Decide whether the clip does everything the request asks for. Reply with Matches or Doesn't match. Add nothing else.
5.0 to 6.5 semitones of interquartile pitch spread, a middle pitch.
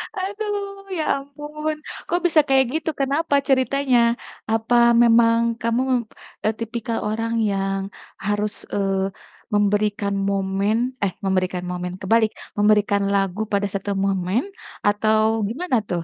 Doesn't match